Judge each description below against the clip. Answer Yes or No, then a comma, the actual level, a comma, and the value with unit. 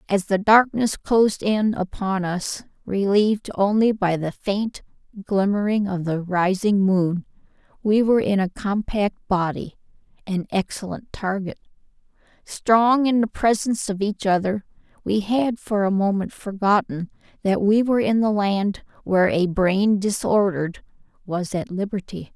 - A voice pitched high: Yes, high, 200 Hz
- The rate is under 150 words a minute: Yes, slow, 135 wpm